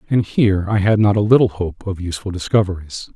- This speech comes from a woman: No, male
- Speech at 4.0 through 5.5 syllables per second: No, 6.1 syllables/s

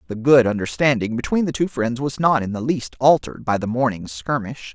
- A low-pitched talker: Yes, low, 125 Hz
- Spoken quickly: Yes, fast, 215 wpm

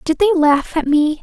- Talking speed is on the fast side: Yes, fast, 245 wpm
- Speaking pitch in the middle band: No, very high, 320 Hz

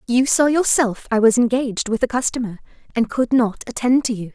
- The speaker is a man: No, female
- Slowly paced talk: No, fast, 205 wpm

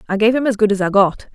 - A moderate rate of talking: No, fast, 355 wpm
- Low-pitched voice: No, high, 210 Hz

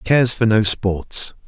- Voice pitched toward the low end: Yes, low, 110 Hz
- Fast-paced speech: No, average, 165 wpm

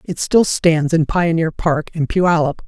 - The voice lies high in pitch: No, medium, 165 Hz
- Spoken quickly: No, average, 180 wpm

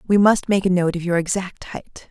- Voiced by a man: No, female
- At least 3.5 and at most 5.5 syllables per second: Yes, 5.0 syllables/s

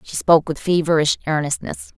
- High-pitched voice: No, medium, 155 Hz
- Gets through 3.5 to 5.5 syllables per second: No, 5.8 syllables/s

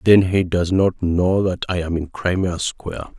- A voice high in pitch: No, very low, 90 Hz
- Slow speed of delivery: No, fast, 205 wpm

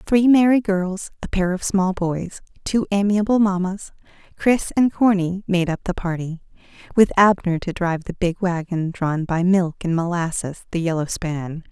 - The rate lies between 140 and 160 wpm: No, average, 170 wpm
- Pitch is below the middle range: No, medium, 185 Hz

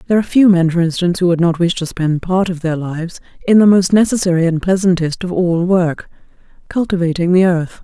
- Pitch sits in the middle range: Yes, medium, 175 Hz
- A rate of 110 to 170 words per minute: No, fast, 205 wpm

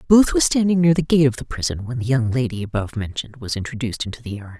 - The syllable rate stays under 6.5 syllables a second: No, 7.0 syllables/s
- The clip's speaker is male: No, female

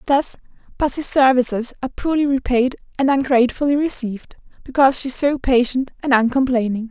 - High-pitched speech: Yes, very high, 260 Hz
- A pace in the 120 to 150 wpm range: Yes, average, 140 wpm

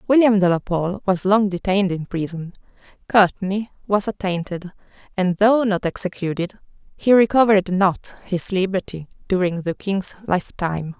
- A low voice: No, high, 190 Hz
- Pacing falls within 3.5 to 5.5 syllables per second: Yes, 4.9 syllables/s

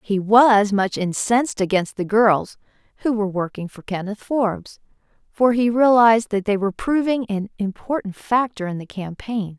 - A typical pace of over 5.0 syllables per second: No, 4.9 syllables/s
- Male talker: No, female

